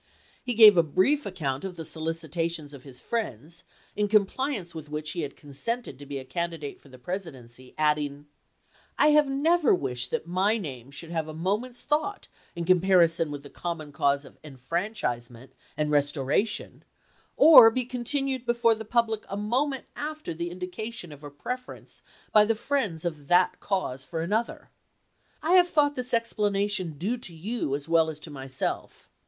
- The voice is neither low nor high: Yes, medium, 175 Hz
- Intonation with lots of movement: Yes, wide, 7.6 semitones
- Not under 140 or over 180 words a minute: Yes, average, 170 wpm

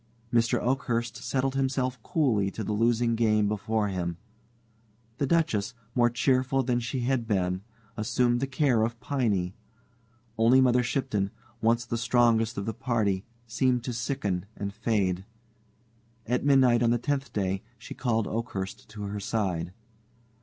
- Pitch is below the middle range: Yes, low, 115 Hz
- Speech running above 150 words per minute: No, average, 145 wpm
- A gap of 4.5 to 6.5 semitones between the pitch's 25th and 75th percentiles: No, average, 3.5 semitones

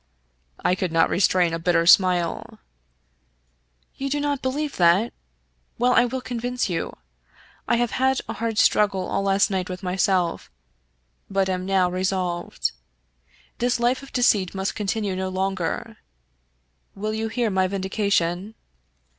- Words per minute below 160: Yes, average, 140 wpm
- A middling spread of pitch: Yes, average, 4.2 semitones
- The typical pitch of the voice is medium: No, high, 195 Hz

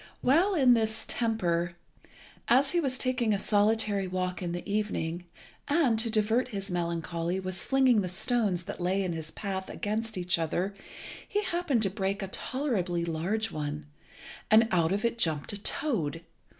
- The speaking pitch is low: No, high, 200 Hz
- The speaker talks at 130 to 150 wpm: No, average, 165 wpm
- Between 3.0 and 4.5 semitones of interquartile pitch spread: No, average, 4.9 semitones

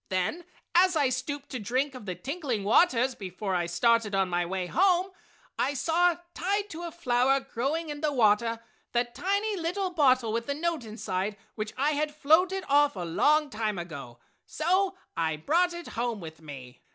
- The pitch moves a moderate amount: No, wide, 8.2 semitones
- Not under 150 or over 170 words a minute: No, average, 180 wpm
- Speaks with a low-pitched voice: No, very high, 260 Hz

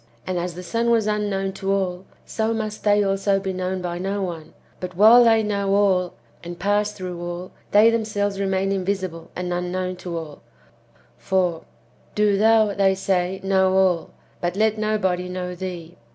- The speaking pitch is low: No, high, 190 Hz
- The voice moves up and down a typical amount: No, narrow, 2.3 semitones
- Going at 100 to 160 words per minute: No, average, 170 wpm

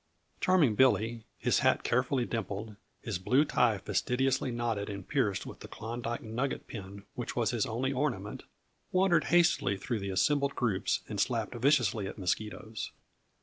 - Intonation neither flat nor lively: Yes, average, 4.2 semitones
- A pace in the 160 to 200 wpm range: No, average, 150 wpm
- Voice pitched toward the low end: Yes, low, 115 Hz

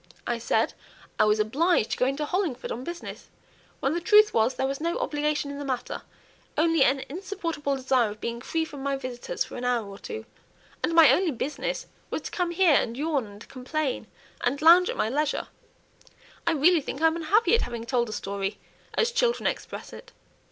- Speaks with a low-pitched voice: No, very high, 285 Hz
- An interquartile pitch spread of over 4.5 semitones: Yes, average, 5.2 semitones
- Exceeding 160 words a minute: Yes, average, 200 wpm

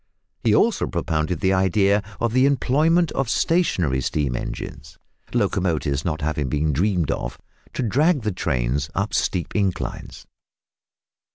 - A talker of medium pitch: No, very low, 95 Hz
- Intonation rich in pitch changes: Yes, wide, 7.6 semitones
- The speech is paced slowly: Yes, slow, 130 wpm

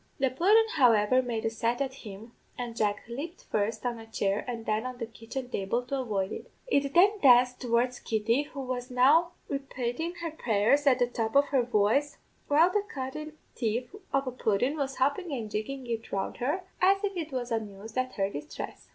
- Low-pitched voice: No, very high, 250 Hz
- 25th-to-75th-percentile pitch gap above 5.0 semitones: No, average, 3.8 semitones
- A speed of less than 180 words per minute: No, average, 200 wpm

